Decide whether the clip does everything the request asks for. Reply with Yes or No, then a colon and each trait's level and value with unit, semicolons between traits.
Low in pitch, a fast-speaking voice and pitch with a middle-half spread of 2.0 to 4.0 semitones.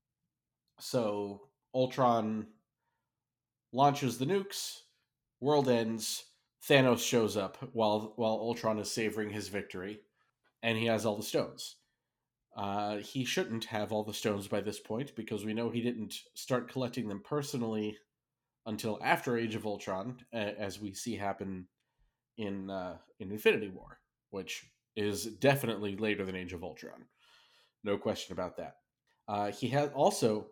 No: low, 110 Hz; average, 145 wpm; average, 3.7 semitones